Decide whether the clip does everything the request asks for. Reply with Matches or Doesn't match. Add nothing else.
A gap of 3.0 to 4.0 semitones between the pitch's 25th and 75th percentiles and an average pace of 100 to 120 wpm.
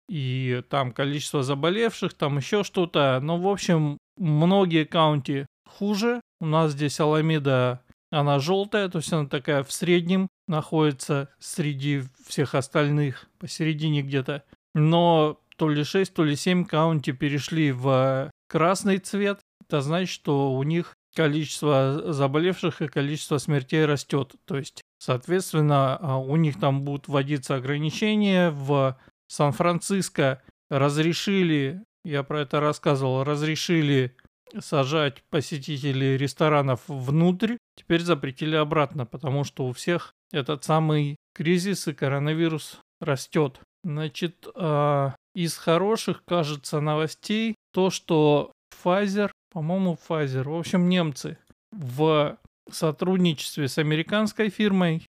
Matches